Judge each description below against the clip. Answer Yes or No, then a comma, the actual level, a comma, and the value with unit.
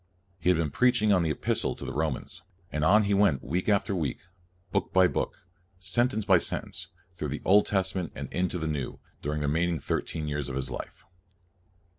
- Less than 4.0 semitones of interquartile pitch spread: No, average, 4.4 semitones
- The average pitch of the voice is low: Yes, very low, 90 Hz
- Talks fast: Yes, fast, 215 wpm